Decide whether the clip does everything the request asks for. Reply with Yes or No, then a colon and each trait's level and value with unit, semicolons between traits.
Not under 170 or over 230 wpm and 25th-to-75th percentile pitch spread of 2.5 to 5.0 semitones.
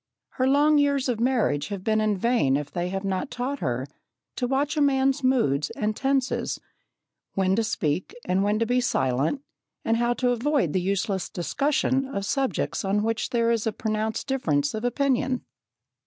No: average, 175 wpm; wide, 5.5 semitones